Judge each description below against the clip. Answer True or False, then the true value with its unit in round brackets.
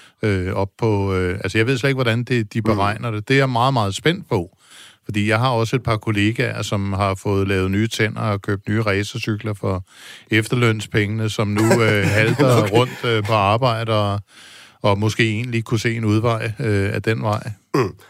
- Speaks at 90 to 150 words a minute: False (195 wpm)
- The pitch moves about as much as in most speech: False (2.2 semitones)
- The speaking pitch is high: False (110 Hz)